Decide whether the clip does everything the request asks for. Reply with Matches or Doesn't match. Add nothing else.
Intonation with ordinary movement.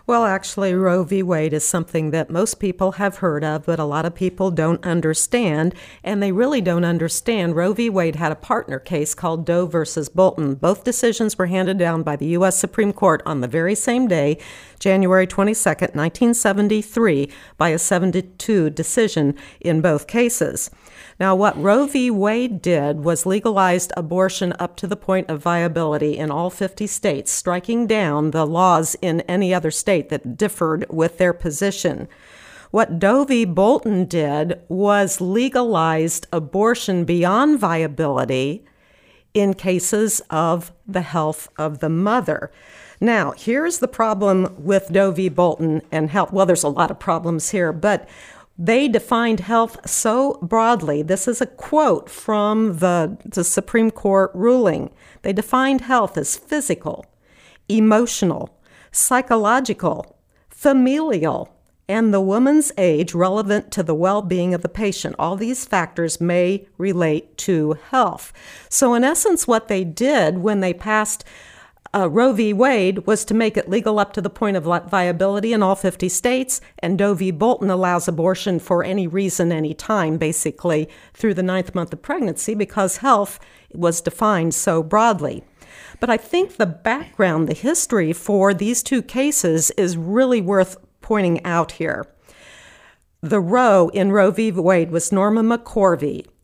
Matches